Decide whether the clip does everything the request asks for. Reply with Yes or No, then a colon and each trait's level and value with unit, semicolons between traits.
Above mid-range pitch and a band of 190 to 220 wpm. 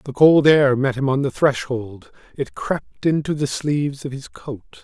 No: low, 135 Hz; average, 200 wpm